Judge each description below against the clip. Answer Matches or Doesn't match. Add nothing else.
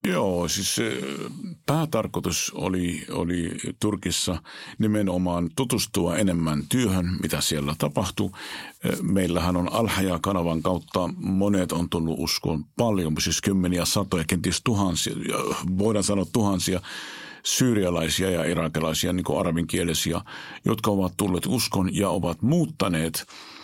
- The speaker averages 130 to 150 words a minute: Doesn't match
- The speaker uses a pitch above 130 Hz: Doesn't match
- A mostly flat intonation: Doesn't match